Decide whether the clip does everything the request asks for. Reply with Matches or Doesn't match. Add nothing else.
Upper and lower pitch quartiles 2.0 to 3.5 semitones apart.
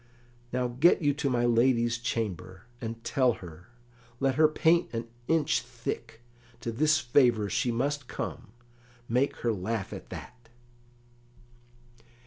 Matches